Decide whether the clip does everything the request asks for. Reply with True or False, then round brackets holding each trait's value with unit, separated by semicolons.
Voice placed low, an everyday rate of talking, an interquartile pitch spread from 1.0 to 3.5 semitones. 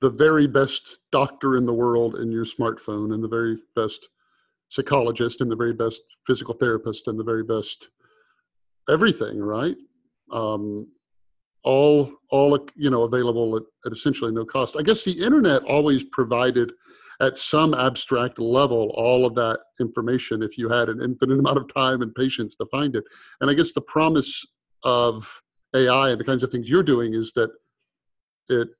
True (120 Hz; 170 wpm; 3.2 semitones)